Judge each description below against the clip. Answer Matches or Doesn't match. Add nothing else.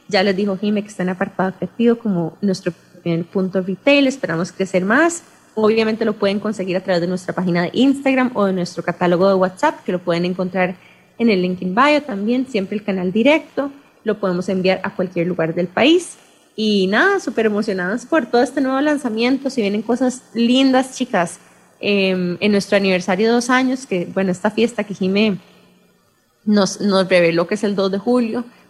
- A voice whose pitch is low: Doesn't match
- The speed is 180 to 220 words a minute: Matches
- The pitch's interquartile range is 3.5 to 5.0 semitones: Matches